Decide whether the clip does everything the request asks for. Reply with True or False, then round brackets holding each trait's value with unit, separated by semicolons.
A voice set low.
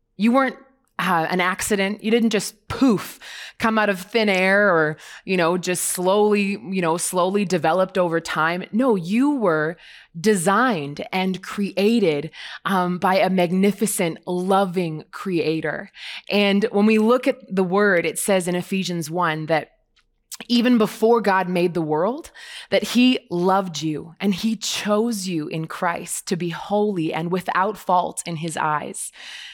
False (190 Hz)